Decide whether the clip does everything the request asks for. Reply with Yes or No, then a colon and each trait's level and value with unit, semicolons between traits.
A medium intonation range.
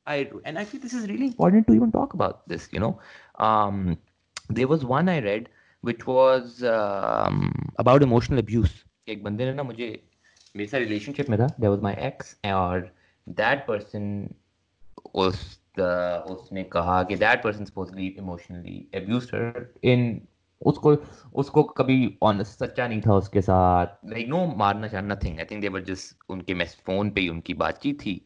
No: wide, 5.7 semitones